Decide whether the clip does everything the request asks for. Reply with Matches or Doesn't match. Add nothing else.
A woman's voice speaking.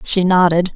Matches